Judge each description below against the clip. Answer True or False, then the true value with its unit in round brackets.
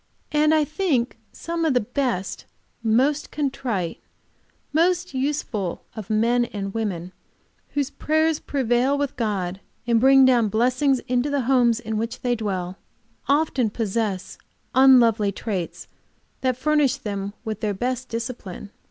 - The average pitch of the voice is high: True (245 Hz)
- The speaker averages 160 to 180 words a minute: False (135 wpm)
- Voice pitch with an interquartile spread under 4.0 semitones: False (4.5 semitones)